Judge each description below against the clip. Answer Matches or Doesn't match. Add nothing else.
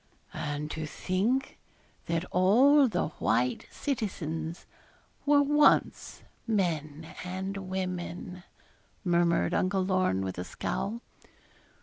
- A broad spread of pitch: Doesn't match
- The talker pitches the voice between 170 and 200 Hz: Matches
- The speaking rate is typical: Doesn't match